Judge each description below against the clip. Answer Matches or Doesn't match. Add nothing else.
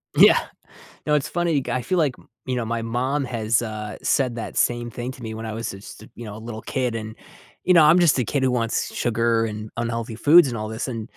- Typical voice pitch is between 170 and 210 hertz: Doesn't match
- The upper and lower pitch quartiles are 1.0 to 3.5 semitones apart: Matches